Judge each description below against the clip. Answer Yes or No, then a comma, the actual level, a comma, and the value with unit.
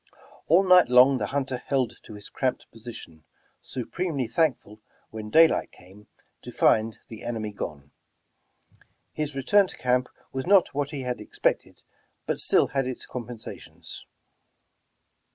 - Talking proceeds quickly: No, average, 140 wpm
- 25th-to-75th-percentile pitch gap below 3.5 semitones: No, average, 4.4 semitones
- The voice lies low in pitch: Yes, low, 125 Hz